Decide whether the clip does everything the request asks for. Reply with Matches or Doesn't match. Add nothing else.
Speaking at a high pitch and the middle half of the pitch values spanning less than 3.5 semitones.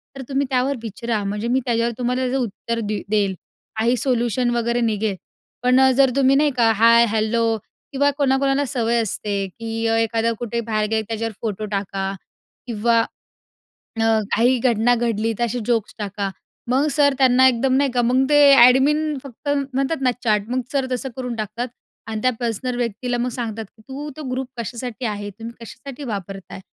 Matches